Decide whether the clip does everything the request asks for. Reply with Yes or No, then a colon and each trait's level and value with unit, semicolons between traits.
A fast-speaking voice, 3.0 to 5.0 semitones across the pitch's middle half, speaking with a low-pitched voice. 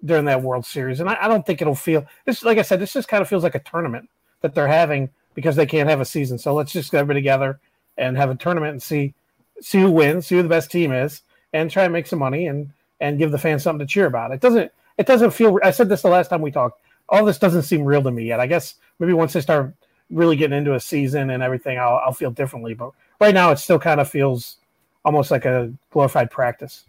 No: fast, 265 wpm; average, 4.4 semitones; medium, 155 Hz